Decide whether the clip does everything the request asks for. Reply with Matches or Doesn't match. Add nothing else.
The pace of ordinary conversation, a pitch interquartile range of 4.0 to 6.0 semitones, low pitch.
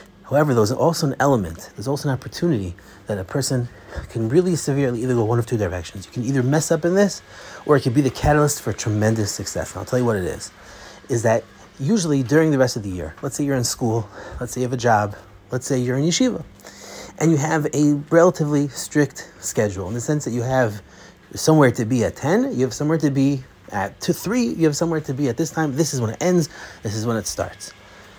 Doesn't match